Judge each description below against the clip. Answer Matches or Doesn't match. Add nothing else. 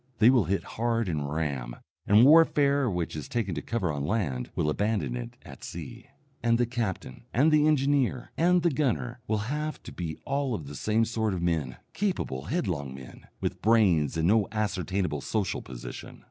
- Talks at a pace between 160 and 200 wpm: Matches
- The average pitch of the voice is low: Matches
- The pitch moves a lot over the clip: Matches